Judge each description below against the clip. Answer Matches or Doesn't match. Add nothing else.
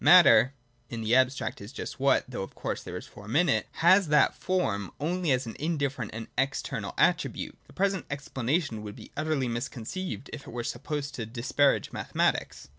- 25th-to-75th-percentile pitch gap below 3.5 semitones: Doesn't match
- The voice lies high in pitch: Doesn't match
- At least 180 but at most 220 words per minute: Matches